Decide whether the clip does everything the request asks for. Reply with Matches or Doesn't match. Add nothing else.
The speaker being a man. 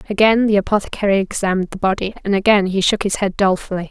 Doesn't match